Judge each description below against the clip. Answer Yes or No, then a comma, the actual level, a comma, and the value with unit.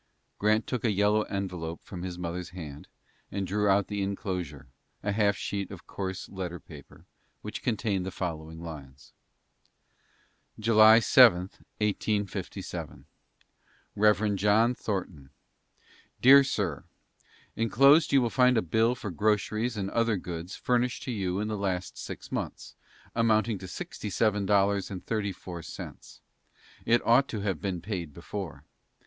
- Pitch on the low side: Yes, low, 100 Hz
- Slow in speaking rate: No, average, 145 wpm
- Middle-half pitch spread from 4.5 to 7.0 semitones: No, average, 3.3 semitones